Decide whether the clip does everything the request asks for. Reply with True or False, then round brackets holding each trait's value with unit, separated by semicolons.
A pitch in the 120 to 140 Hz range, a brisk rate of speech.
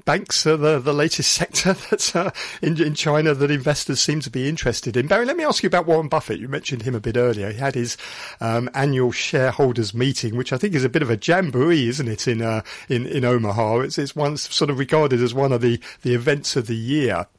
True (135 Hz; 240 wpm)